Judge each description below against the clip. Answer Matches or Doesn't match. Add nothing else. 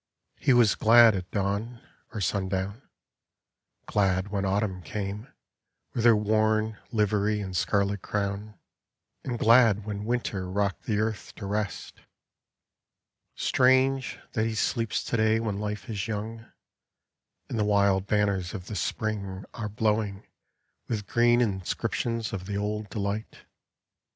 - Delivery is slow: Matches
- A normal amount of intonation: Doesn't match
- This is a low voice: Matches